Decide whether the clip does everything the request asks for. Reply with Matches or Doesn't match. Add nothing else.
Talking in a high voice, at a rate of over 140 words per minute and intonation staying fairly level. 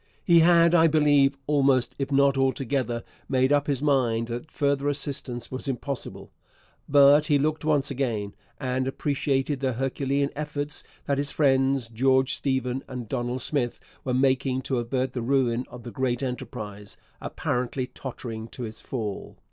Doesn't match